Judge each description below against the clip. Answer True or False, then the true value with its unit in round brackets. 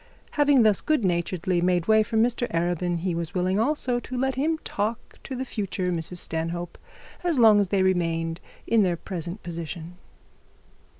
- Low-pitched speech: False (185 Hz)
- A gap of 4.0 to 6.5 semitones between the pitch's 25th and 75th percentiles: True (5.1 semitones)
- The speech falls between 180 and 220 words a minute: False (170 wpm)